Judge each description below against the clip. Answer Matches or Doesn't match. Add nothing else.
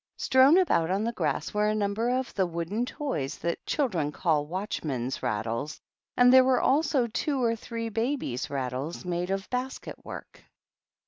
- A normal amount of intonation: Doesn't match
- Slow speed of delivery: Doesn't match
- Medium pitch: Doesn't match